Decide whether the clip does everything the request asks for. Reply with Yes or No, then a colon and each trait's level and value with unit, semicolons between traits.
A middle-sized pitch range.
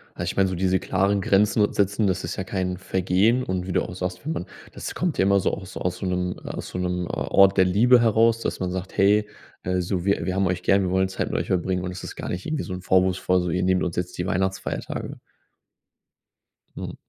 No: narrow, 1.4 semitones